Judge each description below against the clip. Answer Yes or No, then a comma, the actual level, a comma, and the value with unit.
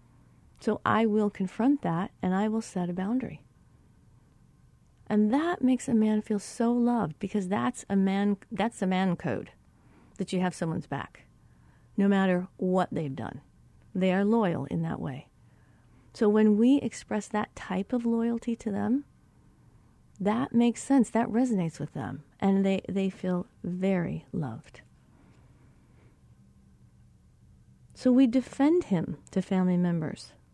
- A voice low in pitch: No, high, 200 Hz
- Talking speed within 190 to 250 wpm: No, average, 145 wpm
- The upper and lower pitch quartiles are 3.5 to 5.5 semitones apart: Yes, average, 4.1 semitones